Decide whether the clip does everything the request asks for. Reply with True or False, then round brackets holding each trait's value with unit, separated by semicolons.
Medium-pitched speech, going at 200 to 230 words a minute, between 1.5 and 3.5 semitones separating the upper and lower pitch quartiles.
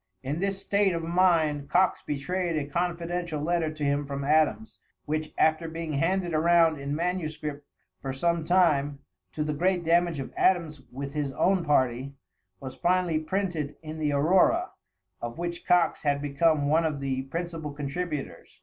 False (155 Hz; 160 wpm; 3.2 semitones)